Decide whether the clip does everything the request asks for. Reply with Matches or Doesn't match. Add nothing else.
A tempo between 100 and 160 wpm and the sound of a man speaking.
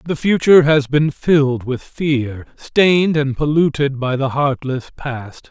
Matches